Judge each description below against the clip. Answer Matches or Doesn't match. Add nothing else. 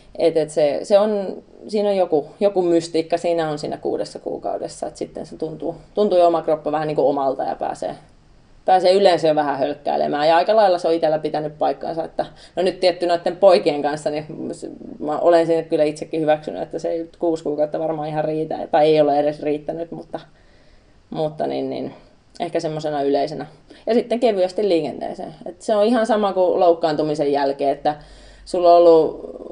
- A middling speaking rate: Doesn't match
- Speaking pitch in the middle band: Matches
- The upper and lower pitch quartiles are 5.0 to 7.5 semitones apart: Doesn't match